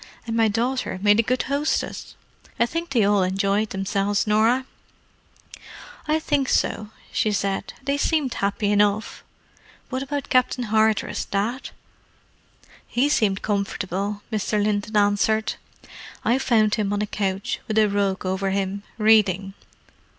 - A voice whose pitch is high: Yes, high, 210 Hz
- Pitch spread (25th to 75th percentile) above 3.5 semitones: No, average, 3.1 semitones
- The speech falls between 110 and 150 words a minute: Yes, slow, 135 wpm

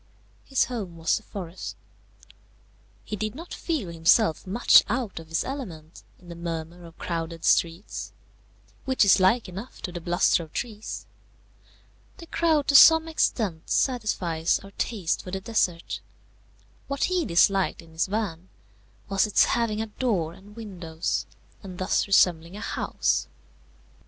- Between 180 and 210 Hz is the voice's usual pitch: Yes, high, 190 Hz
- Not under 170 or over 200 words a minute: No, average, 145 wpm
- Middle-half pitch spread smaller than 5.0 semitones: No, average, 5.3 semitones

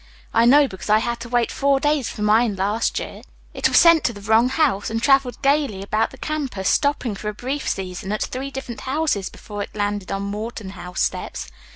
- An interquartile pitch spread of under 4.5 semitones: No, average, 5.0 semitones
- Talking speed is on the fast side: Yes, fast, 215 wpm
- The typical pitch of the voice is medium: No, high, 230 Hz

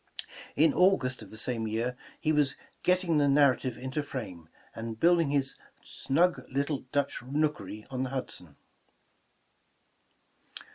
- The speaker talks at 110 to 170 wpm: Yes, slow, 135 wpm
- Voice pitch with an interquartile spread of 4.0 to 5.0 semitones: Yes, average, 4.5 semitones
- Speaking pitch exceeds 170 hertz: No, low, 135 Hz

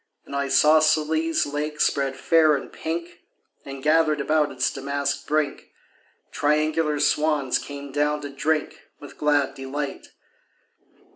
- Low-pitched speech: No, medium, 150 Hz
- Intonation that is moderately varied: No, narrow, 1.8 semitones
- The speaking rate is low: Yes, slow, 120 wpm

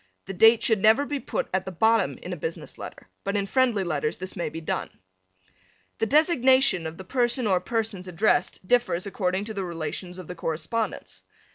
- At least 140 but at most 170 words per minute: No, average, 190 wpm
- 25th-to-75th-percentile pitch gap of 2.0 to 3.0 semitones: No, average, 4.6 semitones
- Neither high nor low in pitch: No, high, 200 Hz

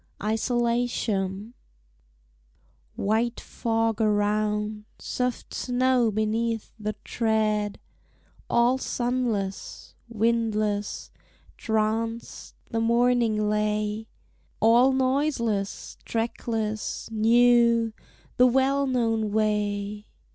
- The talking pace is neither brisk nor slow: No, slow, 75 wpm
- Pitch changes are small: Yes, narrow, 2.1 semitones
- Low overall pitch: No, high, 225 Hz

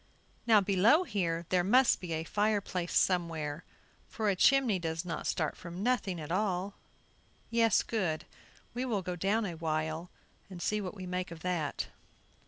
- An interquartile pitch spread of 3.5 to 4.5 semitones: Yes, average, 4.0 semitones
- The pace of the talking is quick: No, average, 170 wpm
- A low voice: No, medium, 185 Hz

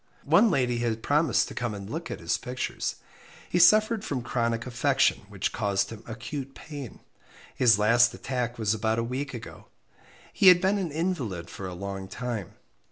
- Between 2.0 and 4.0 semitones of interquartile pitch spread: No, average, 4.8 semitones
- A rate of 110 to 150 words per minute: No, average, 175 wpm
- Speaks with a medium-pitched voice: No, low, 120 Hz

